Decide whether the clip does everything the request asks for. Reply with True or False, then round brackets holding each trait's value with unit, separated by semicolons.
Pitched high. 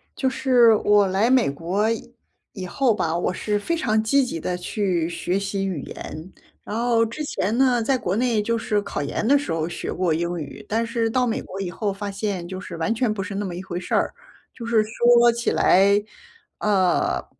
True (205 Hz)